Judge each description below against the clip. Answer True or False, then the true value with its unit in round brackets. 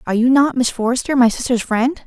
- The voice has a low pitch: False (245 Hz)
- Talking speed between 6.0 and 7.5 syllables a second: True (6.2 syllables/s)